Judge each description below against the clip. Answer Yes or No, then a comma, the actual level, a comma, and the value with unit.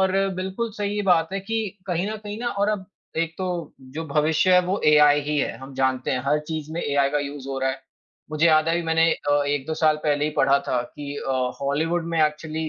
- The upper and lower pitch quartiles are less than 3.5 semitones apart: No, average, 3.9 semitones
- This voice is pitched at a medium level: Yes, medium, 155 Hz